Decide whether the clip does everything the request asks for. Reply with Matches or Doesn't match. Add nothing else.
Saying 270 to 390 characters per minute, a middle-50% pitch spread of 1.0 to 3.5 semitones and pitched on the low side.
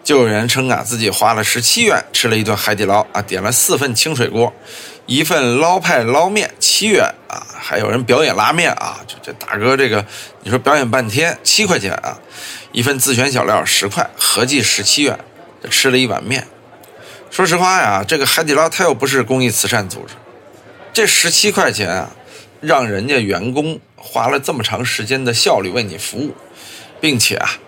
Matches